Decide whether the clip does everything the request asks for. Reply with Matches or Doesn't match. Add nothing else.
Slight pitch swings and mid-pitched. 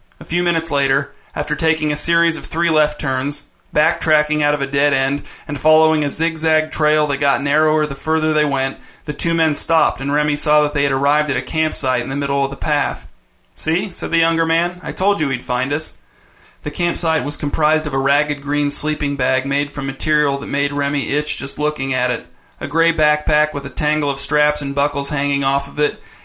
Matches